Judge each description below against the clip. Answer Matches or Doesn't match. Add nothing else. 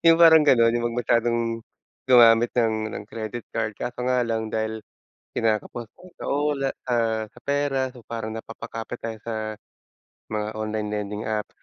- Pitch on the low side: Matches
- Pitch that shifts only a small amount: Matches